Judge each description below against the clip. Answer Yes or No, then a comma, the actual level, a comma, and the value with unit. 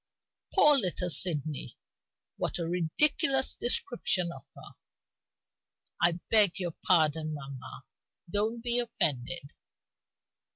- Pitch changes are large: Yes, wide, 6.8 semitones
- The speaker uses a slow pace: Yes, slow, 95 wpm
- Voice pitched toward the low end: No, medium, 175 Hz